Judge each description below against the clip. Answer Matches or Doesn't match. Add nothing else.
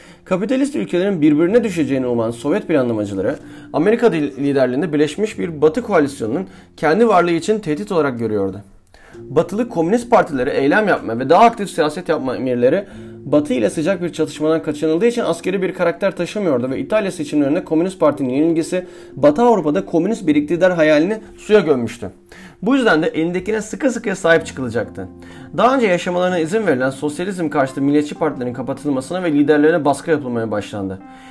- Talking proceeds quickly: Matches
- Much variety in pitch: Matches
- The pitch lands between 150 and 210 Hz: Matches